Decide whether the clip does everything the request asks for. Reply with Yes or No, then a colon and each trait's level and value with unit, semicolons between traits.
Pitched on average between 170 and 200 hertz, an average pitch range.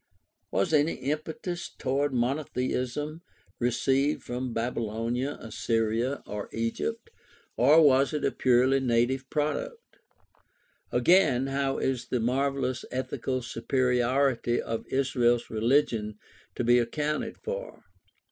No: low, 130 Hz; average, 3.1 semitones